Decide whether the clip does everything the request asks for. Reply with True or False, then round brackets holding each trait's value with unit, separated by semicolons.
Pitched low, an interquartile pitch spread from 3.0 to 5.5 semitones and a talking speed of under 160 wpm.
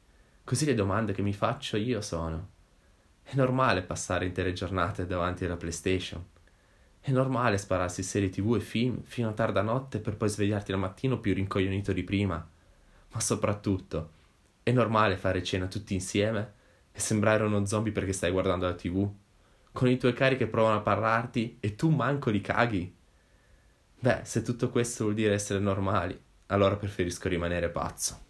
False (100 Hz; 3.5 semitones; 165 wpm)